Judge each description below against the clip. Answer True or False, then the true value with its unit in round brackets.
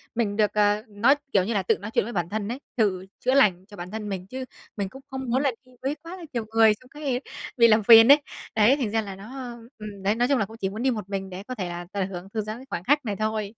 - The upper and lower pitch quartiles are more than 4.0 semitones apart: False (3.7 semitones)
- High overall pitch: True (215 Hz)